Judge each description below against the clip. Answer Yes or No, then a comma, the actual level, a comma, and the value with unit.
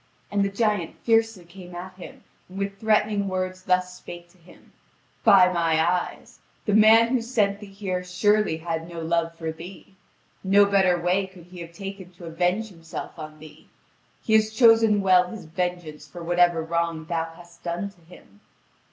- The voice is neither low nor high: Yes, medium, 180 Hz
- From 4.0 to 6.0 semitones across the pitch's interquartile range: No, average, 3.0 semitones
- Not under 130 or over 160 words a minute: No, average, 180 wpm